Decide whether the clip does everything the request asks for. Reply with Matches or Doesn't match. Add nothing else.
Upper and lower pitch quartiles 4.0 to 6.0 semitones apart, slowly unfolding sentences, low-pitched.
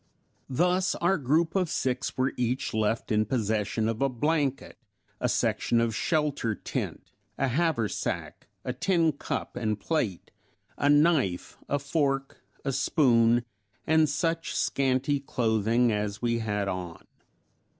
Matches